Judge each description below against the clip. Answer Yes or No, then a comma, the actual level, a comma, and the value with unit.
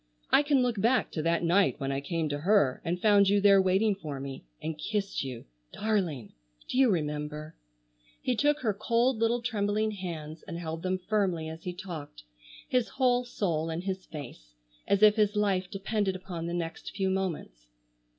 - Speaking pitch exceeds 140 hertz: Yes, medium, 185 Hz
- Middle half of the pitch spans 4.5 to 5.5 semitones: Yes, average, 5.0 semitones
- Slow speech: No, average, 180 wpm